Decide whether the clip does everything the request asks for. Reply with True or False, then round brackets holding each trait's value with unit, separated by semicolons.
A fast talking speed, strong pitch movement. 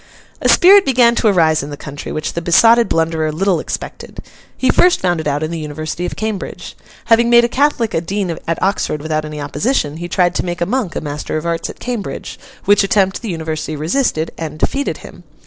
True (215 wpm; 6.4 semitones)